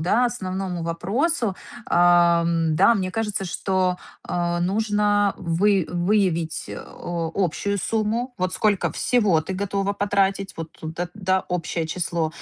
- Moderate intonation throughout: Yes, average, 3.1 semitones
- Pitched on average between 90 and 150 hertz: No, medium, 185 Hz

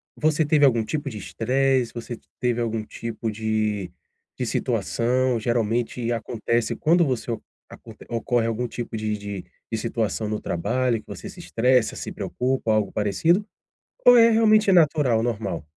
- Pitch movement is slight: No, average, 3.2 semitones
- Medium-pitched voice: No, low, 115 Hz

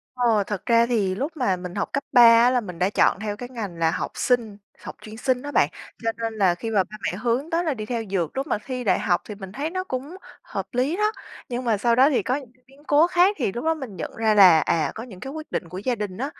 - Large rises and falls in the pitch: No, average, 4.9 semitones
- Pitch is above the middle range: Yes, high, 235 Hz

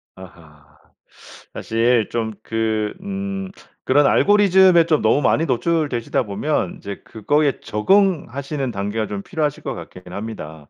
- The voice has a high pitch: No, low, 120 Hz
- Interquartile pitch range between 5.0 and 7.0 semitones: No, wide, 7.4 semitones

